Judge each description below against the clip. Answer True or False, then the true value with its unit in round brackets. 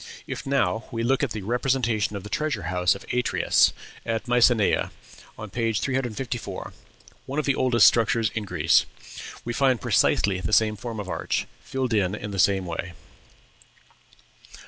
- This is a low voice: True (115 Hz)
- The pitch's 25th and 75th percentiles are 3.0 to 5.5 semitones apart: True (3.7 semitones)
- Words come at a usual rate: True (160 wpm)